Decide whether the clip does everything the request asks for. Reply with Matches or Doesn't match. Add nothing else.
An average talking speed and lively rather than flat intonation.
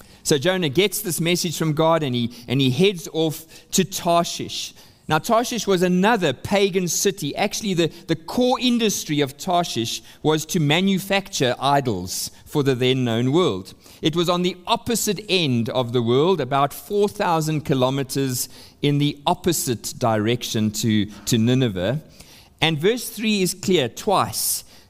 Matches